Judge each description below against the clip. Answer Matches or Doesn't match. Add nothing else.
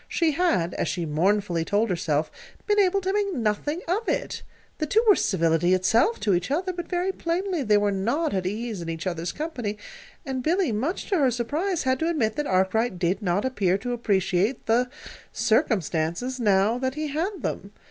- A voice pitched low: Doesn't match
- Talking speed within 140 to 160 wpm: Doesn't match